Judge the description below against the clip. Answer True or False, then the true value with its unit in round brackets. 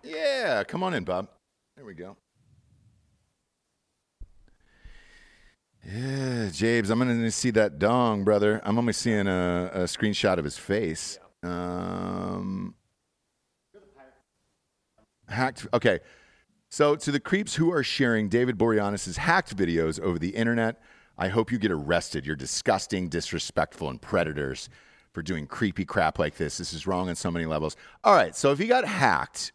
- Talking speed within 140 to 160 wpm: True (150 wpm)